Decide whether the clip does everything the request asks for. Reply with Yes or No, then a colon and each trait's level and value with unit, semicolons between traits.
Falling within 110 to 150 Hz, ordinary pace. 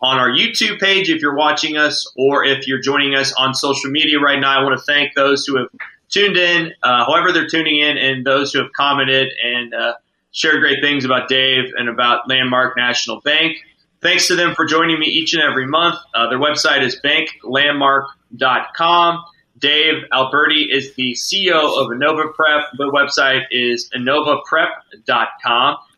Yes: medium, 140 Hz; average, 175 wpm